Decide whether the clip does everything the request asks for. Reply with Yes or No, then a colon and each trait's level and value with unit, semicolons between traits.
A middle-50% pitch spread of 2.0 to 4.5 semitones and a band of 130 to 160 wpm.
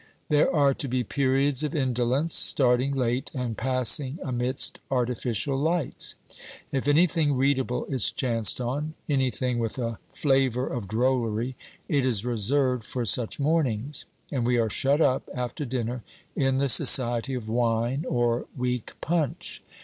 Yes: narrow, 2.6 semitones; average, 140 wpm